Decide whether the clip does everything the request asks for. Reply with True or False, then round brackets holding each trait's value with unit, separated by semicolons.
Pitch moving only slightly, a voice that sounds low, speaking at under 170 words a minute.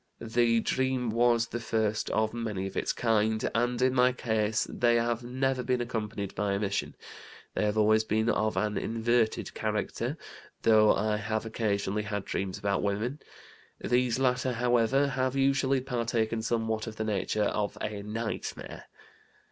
True (2.3 semitones; 115 Hz; 155 wpm)